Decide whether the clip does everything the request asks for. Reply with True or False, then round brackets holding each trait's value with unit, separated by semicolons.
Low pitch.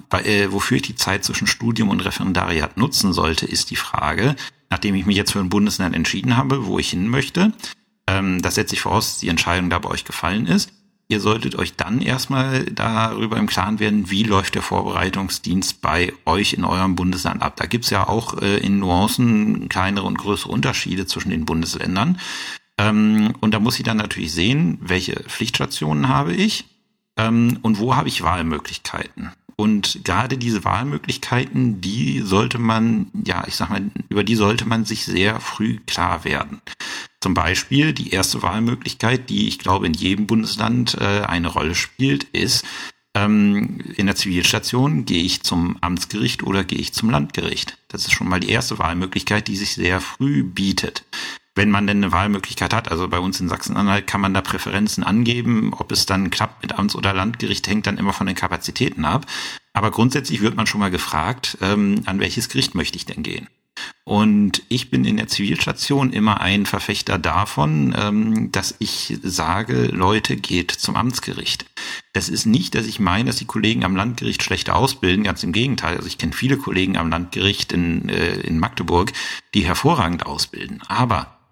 True (105 Hz)